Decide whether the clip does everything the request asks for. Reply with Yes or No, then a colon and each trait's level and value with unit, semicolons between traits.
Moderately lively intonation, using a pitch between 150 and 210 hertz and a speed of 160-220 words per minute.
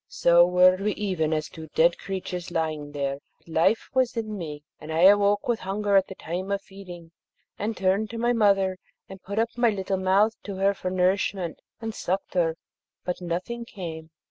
Yes: average, 3.0 semitones; high, 190 Hz; average, 195 wpm